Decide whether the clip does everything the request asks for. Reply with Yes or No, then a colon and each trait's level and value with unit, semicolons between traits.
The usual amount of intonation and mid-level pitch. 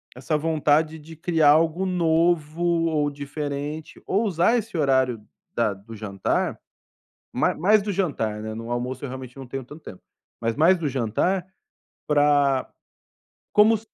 Yes: average, 4.6 semitones; medium, 150 Hz